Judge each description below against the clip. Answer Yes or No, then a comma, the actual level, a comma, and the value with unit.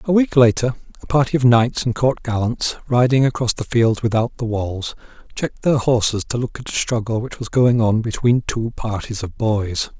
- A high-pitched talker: No, low, 120 Hz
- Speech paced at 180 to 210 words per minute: Yes, fast, 205 wpm